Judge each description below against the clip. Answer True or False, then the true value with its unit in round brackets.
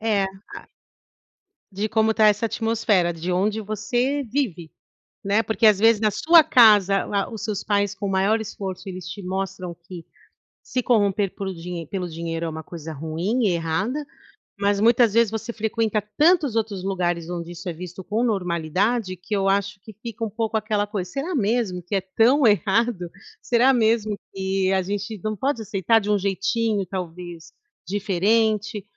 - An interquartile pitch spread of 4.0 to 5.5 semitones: False (3.3 semitones)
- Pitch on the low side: False (205 Hz)